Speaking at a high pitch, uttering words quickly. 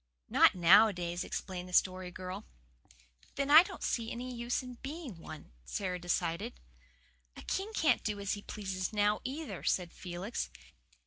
No: high, 200 Hz; average, 150 wpm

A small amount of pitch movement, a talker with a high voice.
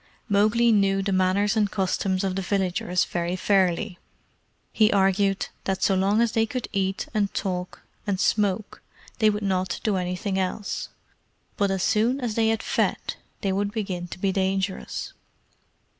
Yes: narrow, 2.0 semitones; high, 195 Hz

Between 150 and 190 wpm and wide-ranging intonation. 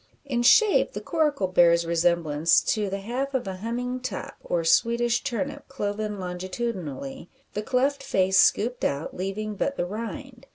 Yes: average, 155 wpm; wide, 5.8 semitones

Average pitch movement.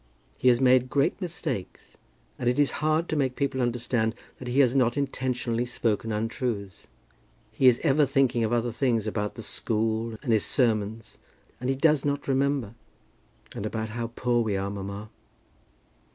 Yes: average, 3.3 semitones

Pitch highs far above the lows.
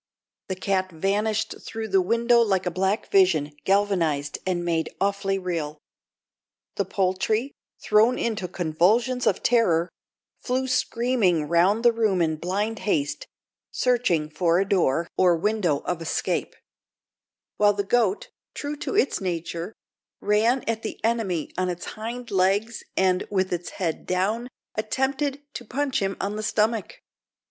No: average, 4.2 semitones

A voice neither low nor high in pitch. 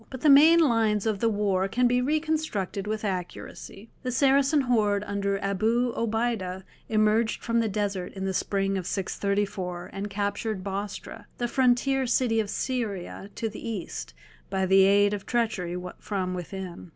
No: high, 210 Hz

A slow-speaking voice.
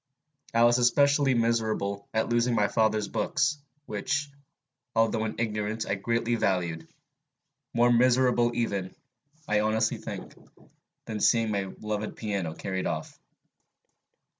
Yes: slow, 125 wpm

